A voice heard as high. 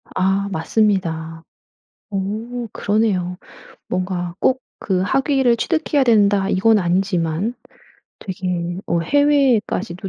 Yes: high, 195 Hz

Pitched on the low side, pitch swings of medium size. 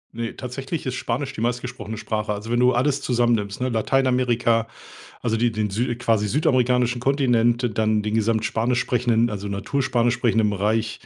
No: low, 120 Hz; narrow, 2.2 semitones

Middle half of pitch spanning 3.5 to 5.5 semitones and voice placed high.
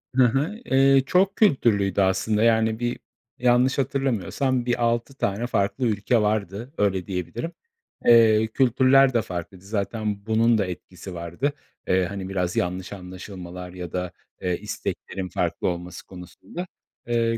No: average, 4.8 semitones; low, 110 Hz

